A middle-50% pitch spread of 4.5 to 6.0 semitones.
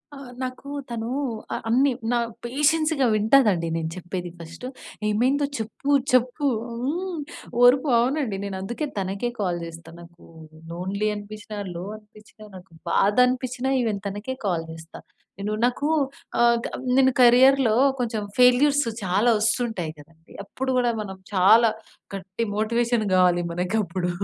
Yes: average, 5.1 semitones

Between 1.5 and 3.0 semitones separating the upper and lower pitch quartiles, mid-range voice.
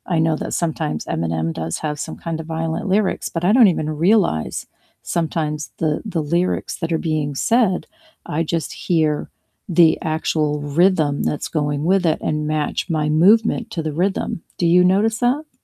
No: average, 3.6 semitones; medium, 160 Hz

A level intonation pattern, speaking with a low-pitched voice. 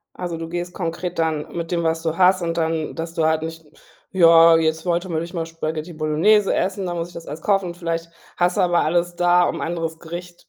No: narrow, 1.3 semitones; medium, 170 Hz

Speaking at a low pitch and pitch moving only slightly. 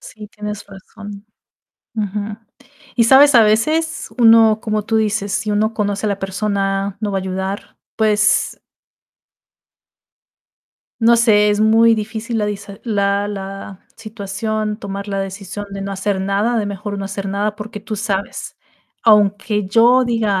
No: high, 210 Hz; narrow, 1.7 semitones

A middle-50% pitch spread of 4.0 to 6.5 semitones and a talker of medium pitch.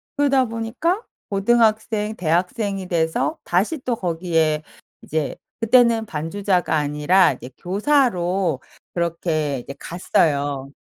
Yes: wide, 6.0 semitones; medium, 180 Hz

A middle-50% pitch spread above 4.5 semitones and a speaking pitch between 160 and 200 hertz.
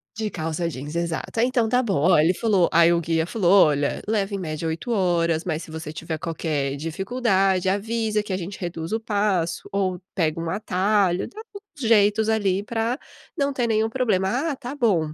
Yes: average, 5.0 semitones; high, 190 Hz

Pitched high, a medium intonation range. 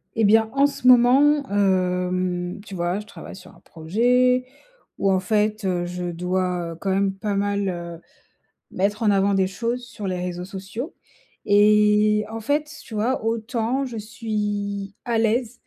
Yes: high, 205 Hz; average, 3.5 semitones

